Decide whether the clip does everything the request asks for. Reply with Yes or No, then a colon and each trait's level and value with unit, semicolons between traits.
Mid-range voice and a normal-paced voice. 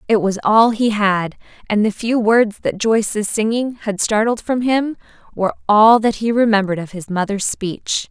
No: high, 215 Hz; average, 185 wpm